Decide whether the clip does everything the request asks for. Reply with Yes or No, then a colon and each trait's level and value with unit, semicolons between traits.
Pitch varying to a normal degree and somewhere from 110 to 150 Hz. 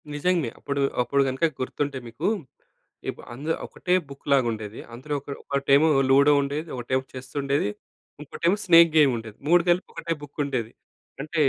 Yes: average, 3.2 semitones; medium, 140 Hz